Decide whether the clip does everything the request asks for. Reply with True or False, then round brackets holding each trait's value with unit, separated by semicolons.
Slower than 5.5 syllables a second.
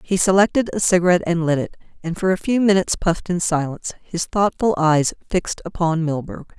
False (5.9 syllables/s)